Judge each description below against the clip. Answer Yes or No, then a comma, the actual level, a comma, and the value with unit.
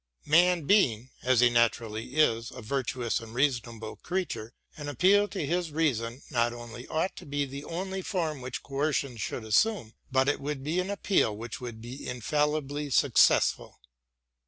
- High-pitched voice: No, low, 135 Hz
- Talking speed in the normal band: Yes, average, 160 wpm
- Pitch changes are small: No, average, 4.9 semitones